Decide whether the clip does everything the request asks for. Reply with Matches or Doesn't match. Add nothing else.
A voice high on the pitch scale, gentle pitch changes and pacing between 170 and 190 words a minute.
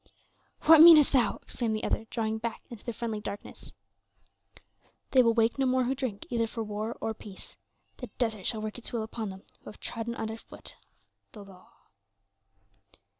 Matches